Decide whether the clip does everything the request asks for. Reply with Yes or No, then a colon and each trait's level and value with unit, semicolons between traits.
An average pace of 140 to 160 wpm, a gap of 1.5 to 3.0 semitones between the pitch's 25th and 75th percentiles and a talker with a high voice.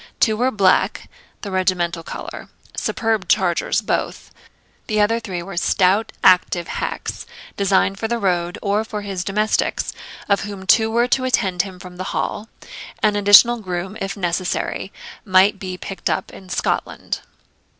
Yes: average, 150 wpm; average, 2.7 semitones; high, 195 Hz